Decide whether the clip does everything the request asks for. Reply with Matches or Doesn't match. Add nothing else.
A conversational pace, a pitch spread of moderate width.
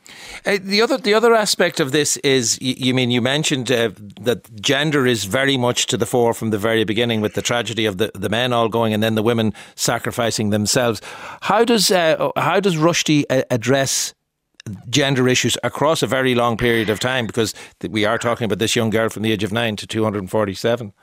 Doesn't match